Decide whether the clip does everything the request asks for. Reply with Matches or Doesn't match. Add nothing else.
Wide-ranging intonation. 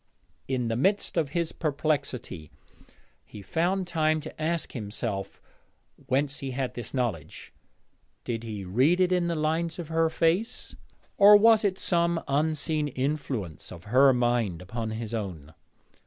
Matches